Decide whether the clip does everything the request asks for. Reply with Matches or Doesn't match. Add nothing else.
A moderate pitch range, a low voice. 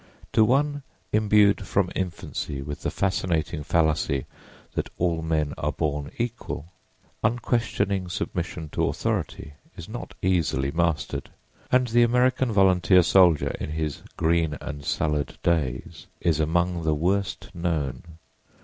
Matches